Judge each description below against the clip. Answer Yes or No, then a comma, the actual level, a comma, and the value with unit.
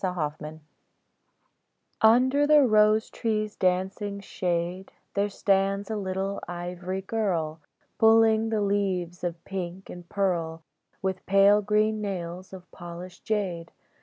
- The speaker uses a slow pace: Yes, slow, 120 wpm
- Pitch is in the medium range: No, high, 195 Hz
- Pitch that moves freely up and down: No, average, 3.1 semitones